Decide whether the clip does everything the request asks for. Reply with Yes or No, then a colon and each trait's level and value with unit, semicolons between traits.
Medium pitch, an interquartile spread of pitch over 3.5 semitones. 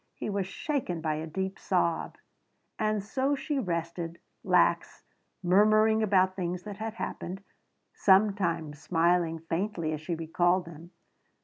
Yes: medium, 180 Hz; average, 3.9 semitones